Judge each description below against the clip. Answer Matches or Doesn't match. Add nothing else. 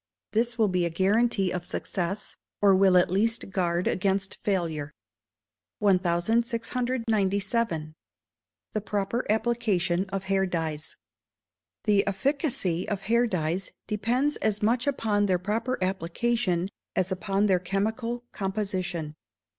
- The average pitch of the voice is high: Matches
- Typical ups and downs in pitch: Matches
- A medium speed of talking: Doesn't match